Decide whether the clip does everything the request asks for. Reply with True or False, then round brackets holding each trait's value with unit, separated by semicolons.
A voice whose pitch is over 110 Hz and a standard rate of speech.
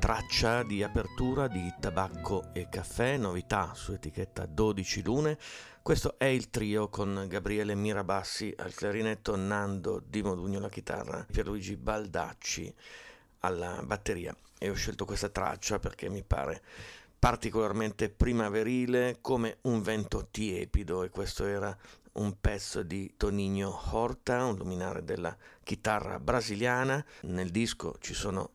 False (105 Hz; 130 wpm)